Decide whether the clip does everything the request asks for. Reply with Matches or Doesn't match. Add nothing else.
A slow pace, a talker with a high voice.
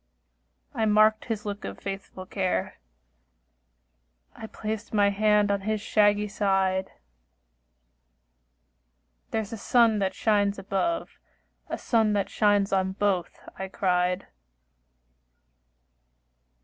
Matches